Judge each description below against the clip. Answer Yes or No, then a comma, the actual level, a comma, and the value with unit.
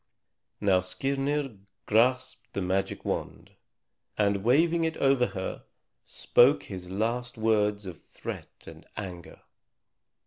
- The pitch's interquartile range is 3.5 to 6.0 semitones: Yes, wide, 5.6 semitones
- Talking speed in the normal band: No, slow, 110 wpm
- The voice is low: Yes, low, 110 Hz